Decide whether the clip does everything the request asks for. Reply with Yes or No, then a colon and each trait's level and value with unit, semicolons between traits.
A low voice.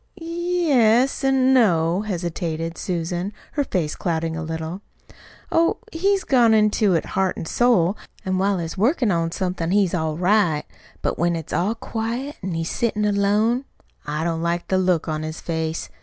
No: medium, 185 Hz